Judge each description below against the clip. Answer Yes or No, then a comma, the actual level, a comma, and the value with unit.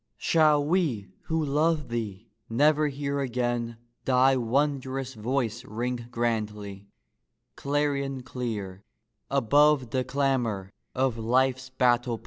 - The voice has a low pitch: Yes, low, 130 Hz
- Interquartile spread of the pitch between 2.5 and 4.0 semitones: Yes, average, 3.3 semitones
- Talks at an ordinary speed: No, slow, 110 wpm